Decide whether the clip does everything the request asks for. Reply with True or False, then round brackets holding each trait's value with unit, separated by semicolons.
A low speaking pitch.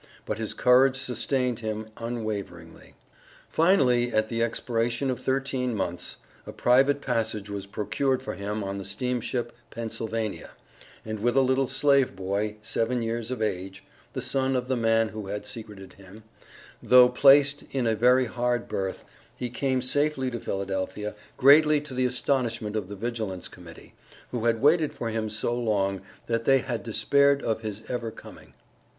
True (115 Hz)